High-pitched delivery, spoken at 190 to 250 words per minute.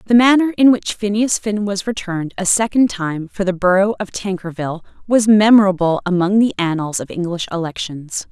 No: high, 195 Hz; average, 175 wpm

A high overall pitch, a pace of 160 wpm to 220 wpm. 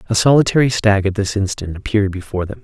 No: low, 100 Hz; fast, 205 wpm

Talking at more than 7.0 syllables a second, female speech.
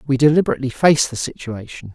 No: 7.3 syllables/s; male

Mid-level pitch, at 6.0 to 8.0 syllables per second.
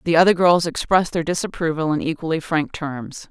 No: medium, 160 Hz; 5.7 syllables/s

